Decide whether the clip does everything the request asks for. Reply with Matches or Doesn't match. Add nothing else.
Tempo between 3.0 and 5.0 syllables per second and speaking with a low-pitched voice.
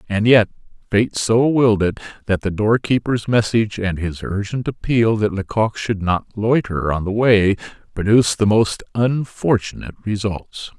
Matches